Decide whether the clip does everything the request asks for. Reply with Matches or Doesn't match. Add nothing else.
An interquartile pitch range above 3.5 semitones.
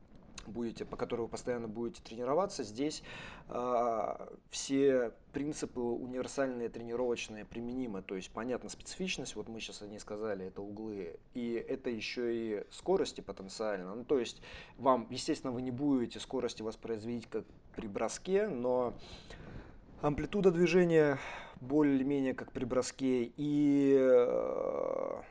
Matches